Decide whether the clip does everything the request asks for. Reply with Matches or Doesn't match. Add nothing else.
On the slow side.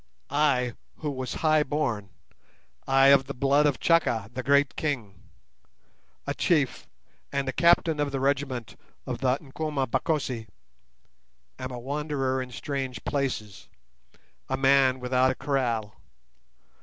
Matches